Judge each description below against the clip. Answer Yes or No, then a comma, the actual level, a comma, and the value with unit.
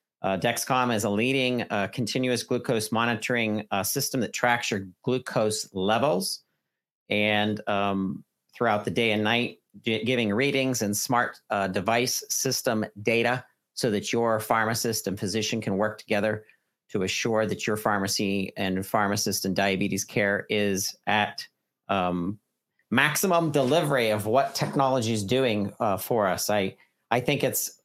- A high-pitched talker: No, low, 110 Hz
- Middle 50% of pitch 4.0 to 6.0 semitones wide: No, average, 3.2 semitones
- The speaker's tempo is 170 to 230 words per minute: No, average, 145 wpm